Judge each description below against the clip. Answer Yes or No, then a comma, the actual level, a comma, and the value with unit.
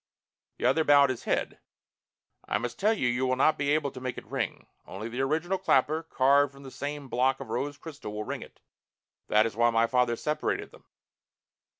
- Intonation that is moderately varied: Yes, average, 3.2 semitones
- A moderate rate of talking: No, fast, 215 wpm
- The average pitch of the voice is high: No, low, 135 Hz